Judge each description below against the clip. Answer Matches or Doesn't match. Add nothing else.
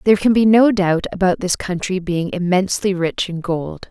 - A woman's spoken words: Matches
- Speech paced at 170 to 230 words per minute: Matches